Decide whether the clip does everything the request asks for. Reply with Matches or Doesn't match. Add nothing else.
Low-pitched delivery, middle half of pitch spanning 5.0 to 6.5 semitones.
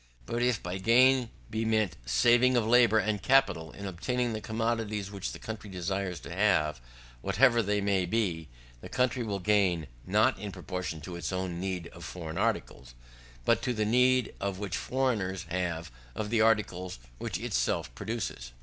Doesn't match